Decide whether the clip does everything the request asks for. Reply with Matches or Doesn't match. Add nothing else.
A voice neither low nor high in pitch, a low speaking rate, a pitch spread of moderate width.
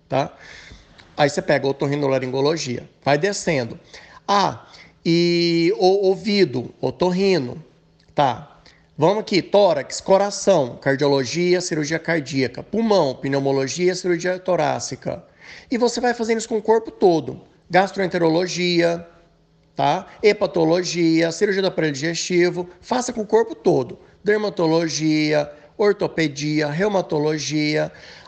Matches